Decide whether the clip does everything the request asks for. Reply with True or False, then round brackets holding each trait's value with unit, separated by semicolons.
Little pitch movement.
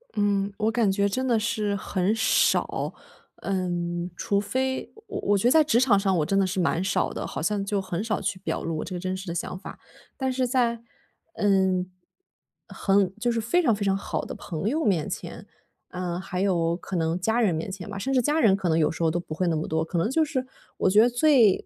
False (4.0 semitones)